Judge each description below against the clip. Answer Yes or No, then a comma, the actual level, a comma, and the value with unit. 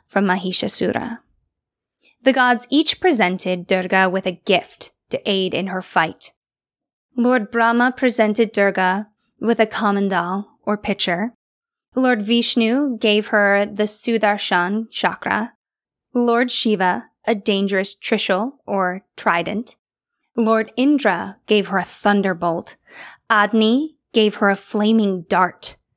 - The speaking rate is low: Yes, slow, 115 wpm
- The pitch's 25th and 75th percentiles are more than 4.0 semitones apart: No, average, 3.6 semitones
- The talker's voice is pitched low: No, high, 210 Hz